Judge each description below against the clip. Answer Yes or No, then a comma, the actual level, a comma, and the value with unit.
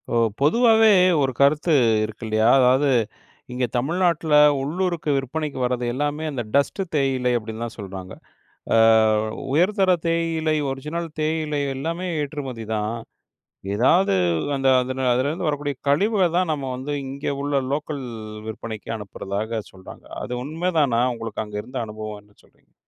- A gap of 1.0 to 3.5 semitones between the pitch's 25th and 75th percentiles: No, average, 5.3 semitones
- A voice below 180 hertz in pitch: Yes, medium, 140 Hz